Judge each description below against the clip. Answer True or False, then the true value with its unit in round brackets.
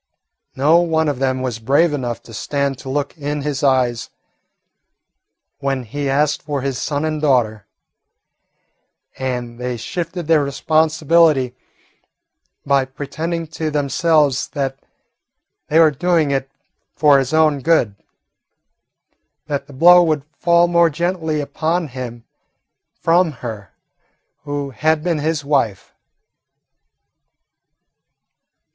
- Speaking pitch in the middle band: True (145 Hz)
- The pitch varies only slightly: False (3.3 semitones)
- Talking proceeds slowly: True (120 wpm)